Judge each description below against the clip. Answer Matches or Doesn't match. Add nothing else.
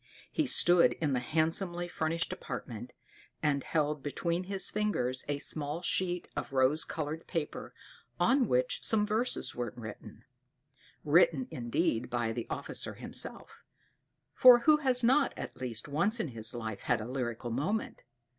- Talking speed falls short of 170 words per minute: Matches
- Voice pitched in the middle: Matches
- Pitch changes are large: Matches